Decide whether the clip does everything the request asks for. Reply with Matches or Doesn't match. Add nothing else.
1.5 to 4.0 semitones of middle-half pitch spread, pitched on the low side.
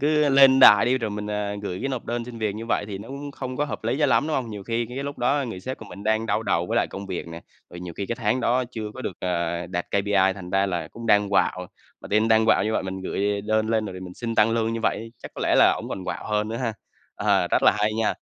Matches